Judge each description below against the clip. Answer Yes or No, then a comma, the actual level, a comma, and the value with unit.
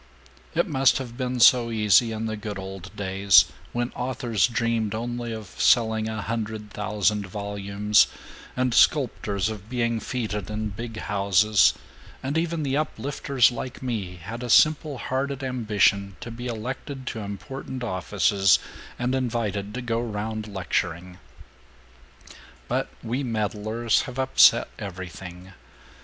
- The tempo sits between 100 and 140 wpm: Yes, slow, 135 wpm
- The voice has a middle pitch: No, low, 110 Hz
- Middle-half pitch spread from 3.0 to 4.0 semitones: Yes, average, 3.5 semitones